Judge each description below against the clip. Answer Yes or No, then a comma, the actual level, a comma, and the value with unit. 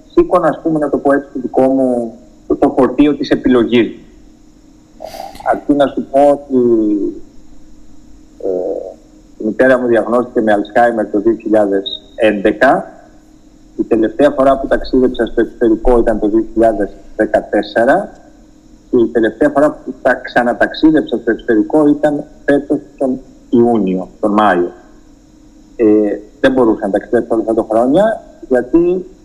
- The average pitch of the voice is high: No, medium, 140 Hz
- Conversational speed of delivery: Yes, average, 130 wpm